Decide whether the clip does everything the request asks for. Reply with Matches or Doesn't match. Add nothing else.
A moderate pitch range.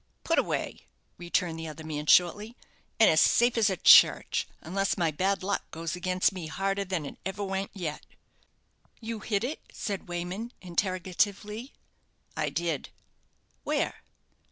Matches